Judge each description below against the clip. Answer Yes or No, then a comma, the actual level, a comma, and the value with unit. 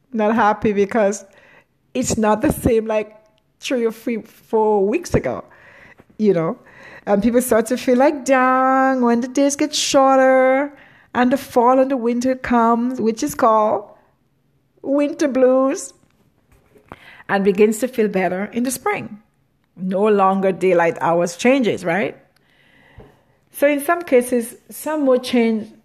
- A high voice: Yes, high, 240 Hz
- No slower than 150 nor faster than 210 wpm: No, average, 140 wpm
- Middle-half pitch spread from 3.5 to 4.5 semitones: Yes, average, 3.8 semitones